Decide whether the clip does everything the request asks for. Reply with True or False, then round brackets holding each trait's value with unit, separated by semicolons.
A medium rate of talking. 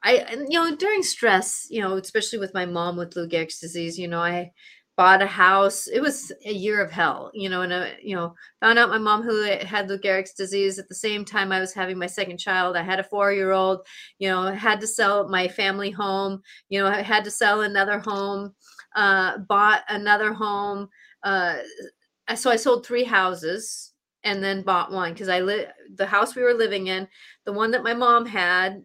False (210 wpm)